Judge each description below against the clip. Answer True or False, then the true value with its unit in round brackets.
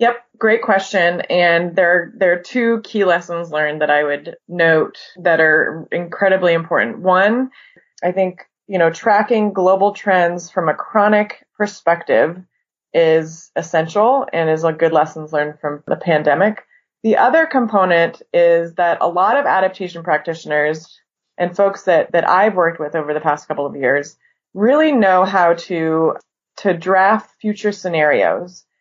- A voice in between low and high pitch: True (175 Hz)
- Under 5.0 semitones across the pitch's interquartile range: True (3.7 semitones)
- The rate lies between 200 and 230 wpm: False (150 wpm)